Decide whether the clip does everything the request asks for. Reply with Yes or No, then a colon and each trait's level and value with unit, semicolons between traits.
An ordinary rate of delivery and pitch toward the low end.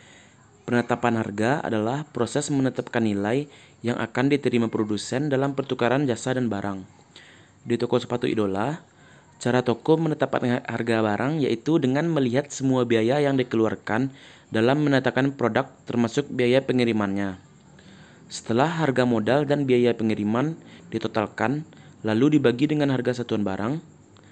Yes: average, 125 wpm; low, 125 Hz